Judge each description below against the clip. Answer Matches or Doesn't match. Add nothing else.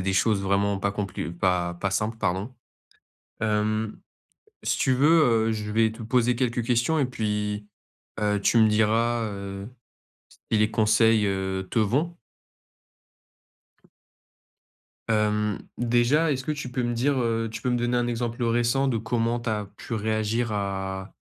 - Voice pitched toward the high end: Doesn't match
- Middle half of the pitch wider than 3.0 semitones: Doesn't match